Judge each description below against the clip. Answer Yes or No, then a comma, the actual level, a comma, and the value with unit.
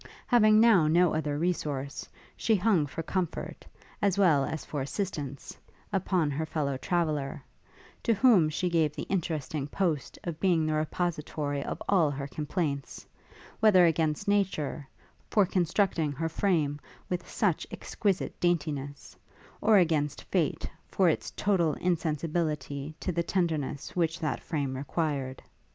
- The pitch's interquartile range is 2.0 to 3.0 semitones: No, average, 3.7 semitones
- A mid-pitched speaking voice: Yes, medium, 160 Hz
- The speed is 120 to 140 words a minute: Yes, slow, 135 wpm